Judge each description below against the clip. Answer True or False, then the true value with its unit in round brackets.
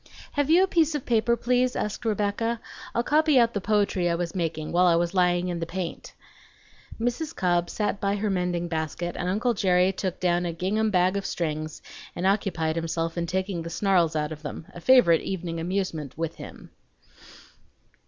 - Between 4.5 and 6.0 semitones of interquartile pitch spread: False (4.0 semitones)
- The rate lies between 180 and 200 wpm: True (190 wpm)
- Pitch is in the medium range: True (180 Hz)